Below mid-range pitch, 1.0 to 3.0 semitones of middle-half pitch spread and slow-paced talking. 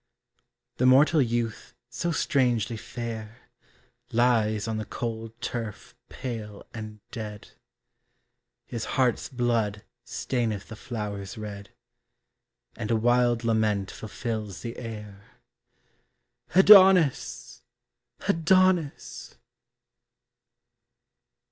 Yes: low, 115 Hz; narrow, 2.6 semitones; slow, 85 wpm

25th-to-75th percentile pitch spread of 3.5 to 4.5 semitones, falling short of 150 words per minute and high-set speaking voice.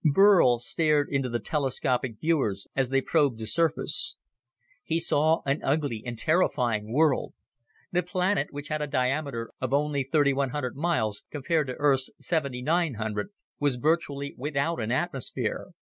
No: average, 3.9 semitones; average, 140 wpm; medium, 140 Hz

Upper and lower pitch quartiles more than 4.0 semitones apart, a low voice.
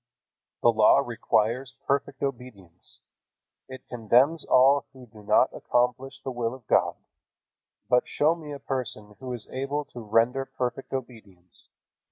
No: average, 2.9 semitones; low, 125 Hz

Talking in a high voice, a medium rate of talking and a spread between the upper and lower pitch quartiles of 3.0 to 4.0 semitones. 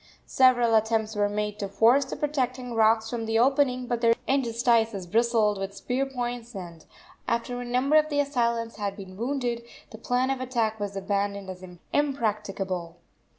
Yes: high, 230 Hz; average, 165 wpm; average, 3.4 semitones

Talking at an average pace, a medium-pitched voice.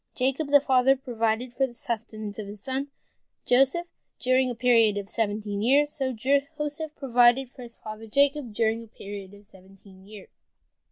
No: average, 175 wpm; high, 240 Hz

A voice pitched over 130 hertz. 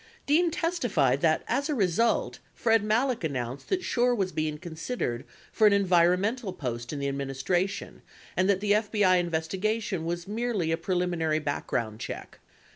Yes: medium, 185 Hz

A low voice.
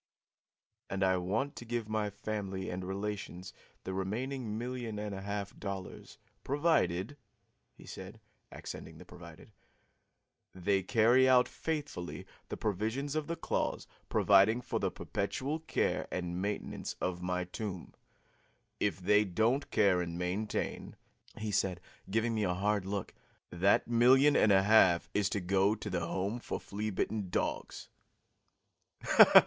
Yes: low, 105 Hz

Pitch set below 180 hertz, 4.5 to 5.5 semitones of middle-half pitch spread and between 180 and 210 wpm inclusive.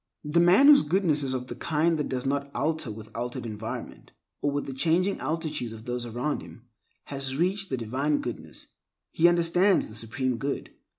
Yes: medium, 140 Hz; average, 5.2 semitones; average, 185 wpm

